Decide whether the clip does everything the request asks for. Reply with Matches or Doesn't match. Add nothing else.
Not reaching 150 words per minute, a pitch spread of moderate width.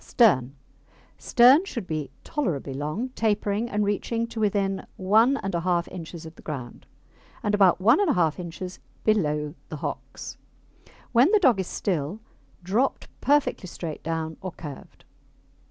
Doesn't match